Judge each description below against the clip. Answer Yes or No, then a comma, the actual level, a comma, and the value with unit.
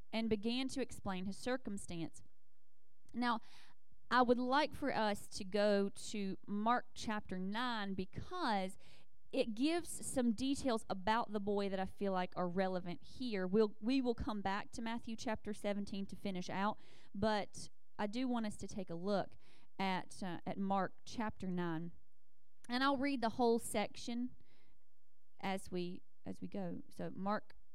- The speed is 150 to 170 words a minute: Yes, average, 160 wpm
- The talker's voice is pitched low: No, high, 210 Hz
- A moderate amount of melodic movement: Yes, average, 3.8 semitones